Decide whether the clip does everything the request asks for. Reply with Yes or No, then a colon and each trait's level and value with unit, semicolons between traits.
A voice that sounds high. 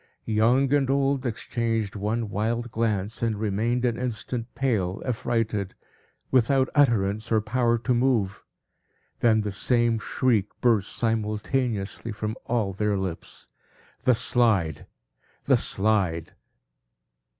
No: low, 115 Hz